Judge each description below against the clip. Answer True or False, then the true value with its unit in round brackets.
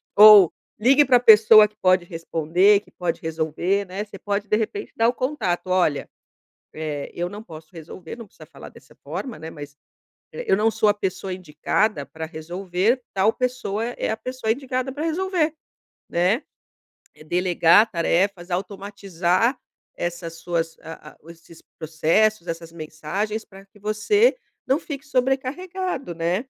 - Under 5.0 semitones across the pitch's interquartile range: False (5.3 semitones)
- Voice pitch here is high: True (195 Hz)